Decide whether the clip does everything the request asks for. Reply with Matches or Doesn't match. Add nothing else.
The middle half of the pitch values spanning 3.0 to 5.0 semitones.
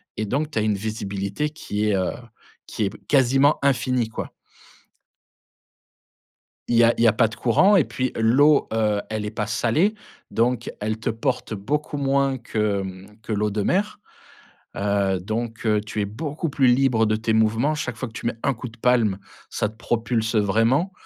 Matches